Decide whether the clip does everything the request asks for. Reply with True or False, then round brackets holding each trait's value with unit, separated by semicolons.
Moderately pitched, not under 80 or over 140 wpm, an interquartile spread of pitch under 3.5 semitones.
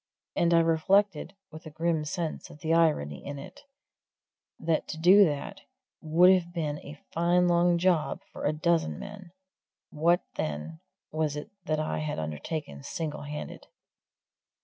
False (160 Hz; 150 wpm; 2.5 semitones)